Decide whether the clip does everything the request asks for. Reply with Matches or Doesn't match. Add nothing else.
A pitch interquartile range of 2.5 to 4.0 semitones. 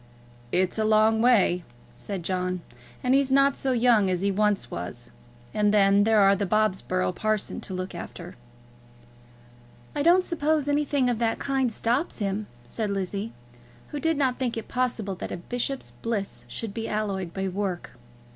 Doesn't match